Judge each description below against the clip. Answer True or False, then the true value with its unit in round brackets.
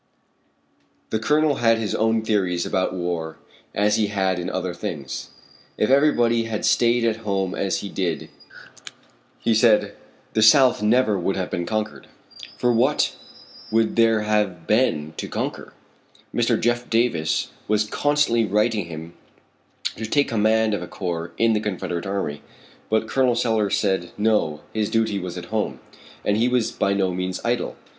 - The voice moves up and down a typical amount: True (3.6 semitones)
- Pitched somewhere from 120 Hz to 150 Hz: False (105 Hz)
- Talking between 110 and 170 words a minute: True (160 wpm)